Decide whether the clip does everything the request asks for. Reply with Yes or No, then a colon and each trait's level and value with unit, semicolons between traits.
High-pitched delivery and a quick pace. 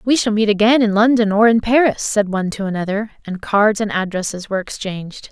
Yes: high, 210 Hz; fast, 215 wpm